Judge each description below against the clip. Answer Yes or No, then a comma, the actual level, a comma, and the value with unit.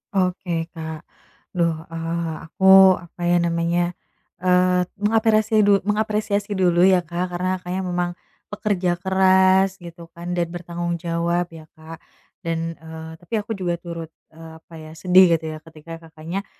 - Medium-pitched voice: Yes, medium, 175 Hz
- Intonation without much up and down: Yes, narrow, 2.2 semitones